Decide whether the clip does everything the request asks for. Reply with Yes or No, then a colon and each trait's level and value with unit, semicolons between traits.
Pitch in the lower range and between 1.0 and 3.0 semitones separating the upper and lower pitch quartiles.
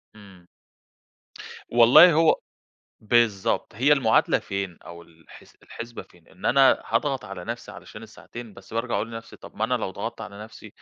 No: low, 115 Hz; average, 3.6 semitones